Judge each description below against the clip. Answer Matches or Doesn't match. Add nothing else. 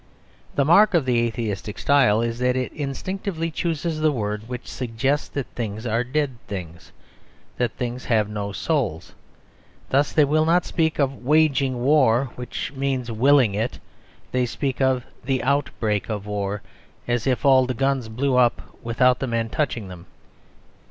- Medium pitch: Doesn't match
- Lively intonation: Doesn't match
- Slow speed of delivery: Doesn't match